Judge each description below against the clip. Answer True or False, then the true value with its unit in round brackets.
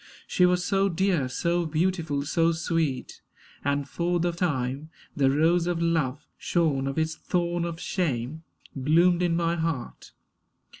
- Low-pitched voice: False (165 Hz)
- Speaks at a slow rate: False (145 wpm)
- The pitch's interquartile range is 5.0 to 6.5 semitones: False (3.3 semitones)